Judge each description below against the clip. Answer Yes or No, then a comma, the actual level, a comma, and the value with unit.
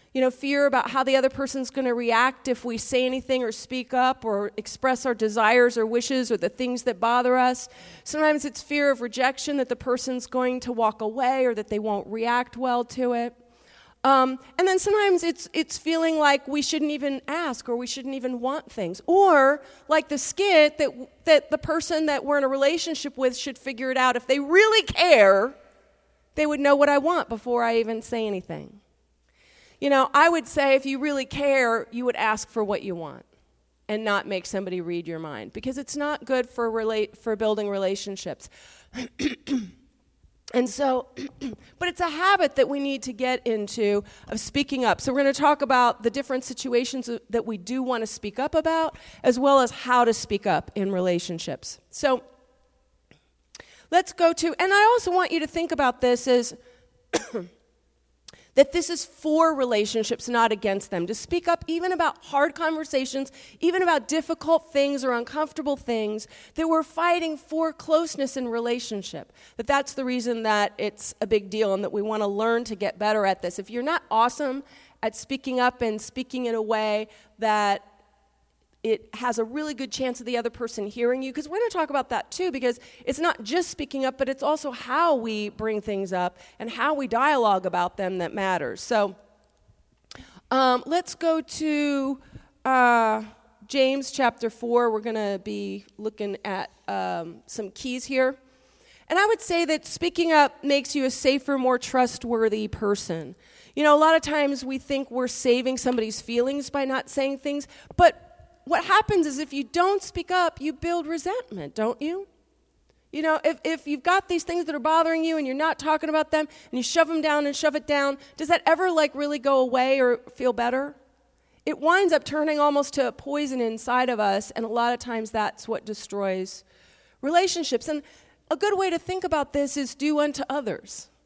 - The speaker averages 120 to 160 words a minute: No, average, 195 wpm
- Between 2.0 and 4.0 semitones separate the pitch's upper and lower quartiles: No, average, 4.6 semitones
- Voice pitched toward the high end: Yes, very high, 260 Hz